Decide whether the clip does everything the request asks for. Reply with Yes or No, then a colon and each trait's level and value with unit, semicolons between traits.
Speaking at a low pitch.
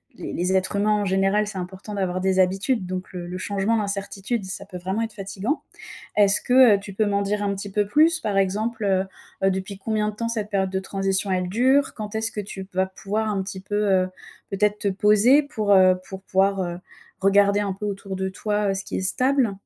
No: high, 200 Hz